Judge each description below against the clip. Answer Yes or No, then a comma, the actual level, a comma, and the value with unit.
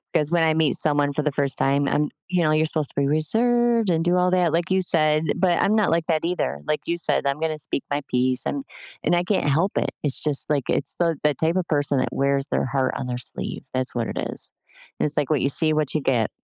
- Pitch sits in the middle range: Yes, medium, 155 Hz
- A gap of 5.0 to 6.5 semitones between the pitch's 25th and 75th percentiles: No, average, 3.6 semitones